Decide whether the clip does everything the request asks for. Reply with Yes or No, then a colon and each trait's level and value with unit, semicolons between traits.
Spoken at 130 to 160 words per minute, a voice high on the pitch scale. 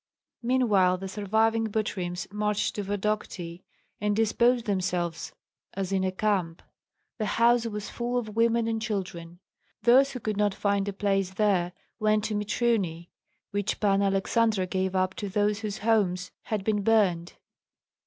Yes: average, 150 wpm; high, 205 Hz